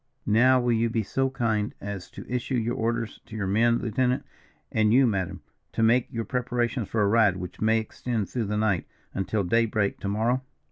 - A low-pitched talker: Yes, low, 115 Hz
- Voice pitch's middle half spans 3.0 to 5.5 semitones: No, narrow, 2.4 semitones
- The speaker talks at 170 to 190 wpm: No, average, 200 wpm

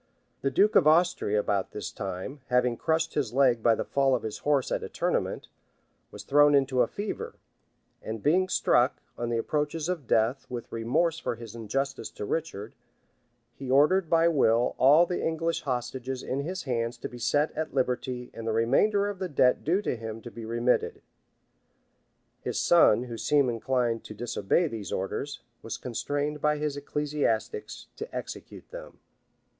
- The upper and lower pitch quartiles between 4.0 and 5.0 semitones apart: Yes, average, 4.7 semitones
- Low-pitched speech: Yes, low, 130 Hz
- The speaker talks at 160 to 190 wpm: Yes, average, 170 wpm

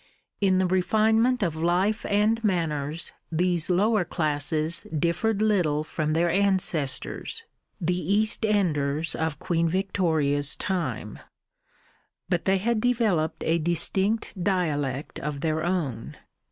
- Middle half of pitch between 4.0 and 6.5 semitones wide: Yes, average, 4.5 semitones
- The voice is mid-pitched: Yes, medium, 175 Hz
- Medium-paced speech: No, slow, 115 wpm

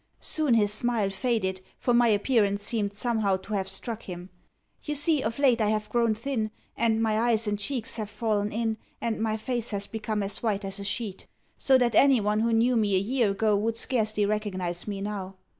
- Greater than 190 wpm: Yes, fast, 205 wpm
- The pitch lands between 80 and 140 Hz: No, high, 215 Hz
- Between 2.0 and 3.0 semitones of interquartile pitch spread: Yes, narrow, 2.5 semitones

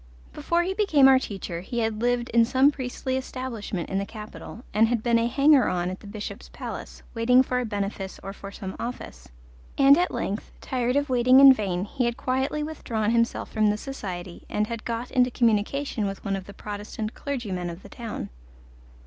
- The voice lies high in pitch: Yes, high, 230 Hz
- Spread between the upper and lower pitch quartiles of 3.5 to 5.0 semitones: Yes, average, 4.2 semitones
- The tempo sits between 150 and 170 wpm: No, average, 200 wpm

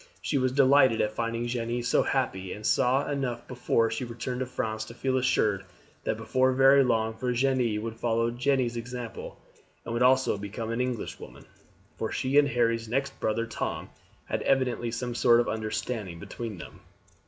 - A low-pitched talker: Yes, low, 120 Hz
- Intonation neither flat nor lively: No, narrow, 2.3 semitones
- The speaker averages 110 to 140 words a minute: No, average, 170 wpm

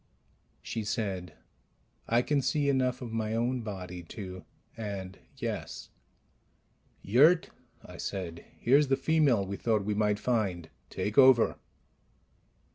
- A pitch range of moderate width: Yes, average, 4.9 semitones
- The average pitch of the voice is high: No, low, 110 Hz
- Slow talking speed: Yes, slow, 125 wpm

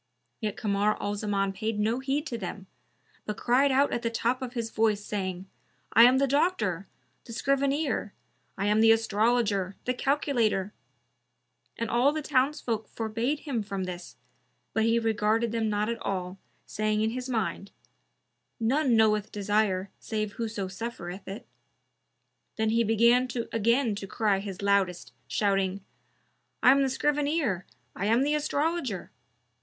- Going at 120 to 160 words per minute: Yes, average, 150 wpm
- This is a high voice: Yes, high, 220 Hz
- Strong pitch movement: No, average, 3.8 semitones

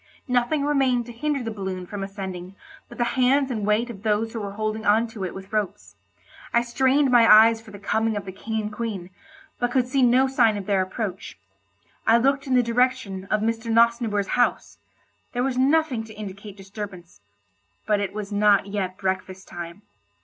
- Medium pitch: No, high, 220 Hz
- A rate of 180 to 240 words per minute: Yes, average, 190 wpm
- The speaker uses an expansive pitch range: No, average, 3.5 semitones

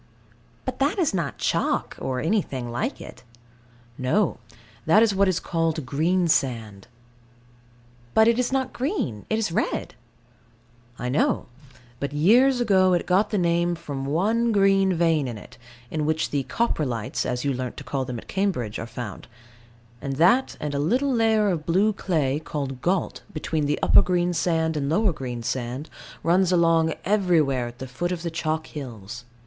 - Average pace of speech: Yes, average, 165 wpm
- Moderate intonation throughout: No, wide, 6.3 semitones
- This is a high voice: No, medium, 165 Hz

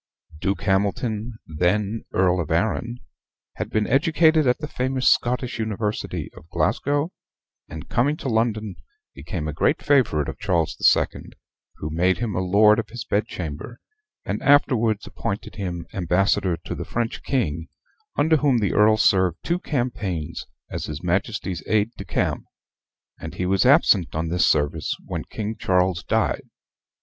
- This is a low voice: Yes, low, 105 Hz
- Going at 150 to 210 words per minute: Yes, average, 155 wpm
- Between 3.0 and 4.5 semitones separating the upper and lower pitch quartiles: No, average, 5.3 semitones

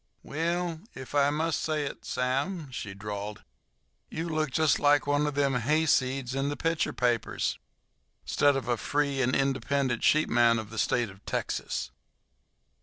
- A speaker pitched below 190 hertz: Yes, medium, 140 Hz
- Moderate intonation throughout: Yes, average, 3.7 semitones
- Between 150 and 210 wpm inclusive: Yes, average, 155 wpm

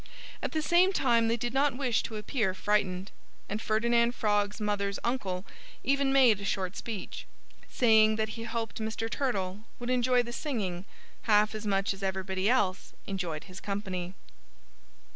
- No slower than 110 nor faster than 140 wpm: No, average, 160 wpm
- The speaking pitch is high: Yes, high, 215 Hz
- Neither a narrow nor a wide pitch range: Yes, average, 3.5 semitones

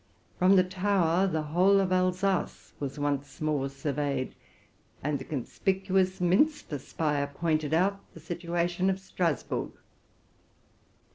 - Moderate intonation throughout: Yes, average, 4.3 semitones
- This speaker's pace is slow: Yes, slow, 120 wpm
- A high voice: No, medium, 175 Hz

